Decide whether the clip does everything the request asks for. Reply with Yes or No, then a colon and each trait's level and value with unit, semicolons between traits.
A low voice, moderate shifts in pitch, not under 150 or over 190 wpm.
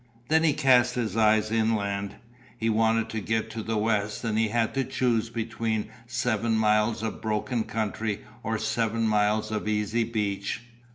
No: low, 110 Hz; narrow, 1.3 semitones; average, 165 wpm